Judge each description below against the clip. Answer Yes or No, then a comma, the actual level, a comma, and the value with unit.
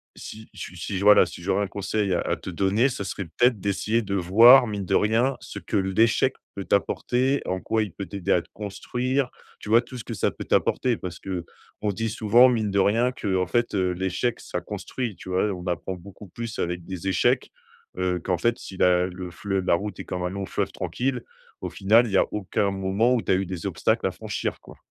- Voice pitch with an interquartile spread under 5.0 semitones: Yes, average, 3.7 semitones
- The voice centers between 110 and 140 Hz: No, low, 100 Hz